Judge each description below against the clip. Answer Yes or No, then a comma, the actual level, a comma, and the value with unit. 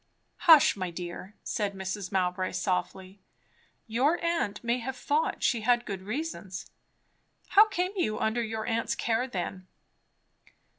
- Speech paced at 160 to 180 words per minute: No, slow, 135 wpm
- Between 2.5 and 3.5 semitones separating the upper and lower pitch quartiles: No, average, 5.1 semitones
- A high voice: Yes, high, 220 Hz